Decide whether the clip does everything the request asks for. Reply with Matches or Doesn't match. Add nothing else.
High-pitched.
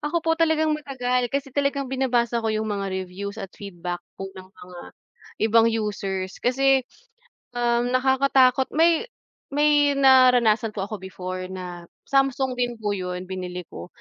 Matches